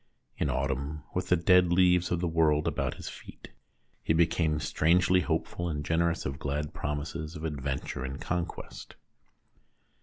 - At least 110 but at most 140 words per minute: No, average, 150 wpm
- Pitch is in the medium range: No, very low, 80 Hz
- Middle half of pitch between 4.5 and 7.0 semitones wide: No, average, 2.8 semitones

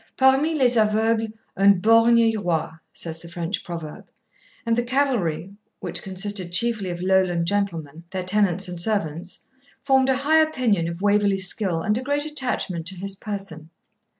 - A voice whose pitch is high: Yes, high, 200 Hz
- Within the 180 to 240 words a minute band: No, average, 160 wpm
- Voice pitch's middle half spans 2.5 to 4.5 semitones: No, average, 5.0 semitones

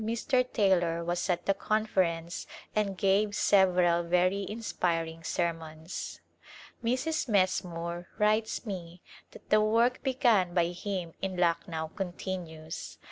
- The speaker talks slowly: Yes, slow, 115 wpm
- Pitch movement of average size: Yes, average, 3.8 semitones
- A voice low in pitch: No, medium, 185 Hz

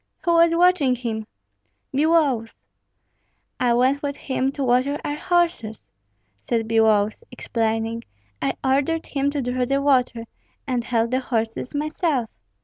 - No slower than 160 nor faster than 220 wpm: No, slow, 135 wpm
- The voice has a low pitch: No, very high, 260 Hz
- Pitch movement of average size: Yes, average, 4.1 semitones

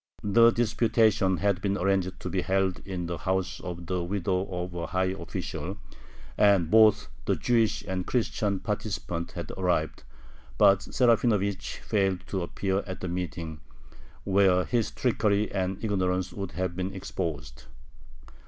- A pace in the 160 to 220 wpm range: No, average, 145 wpm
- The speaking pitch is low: Yes, very low, 95 Hz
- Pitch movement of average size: No, narrow, 2.2 semitones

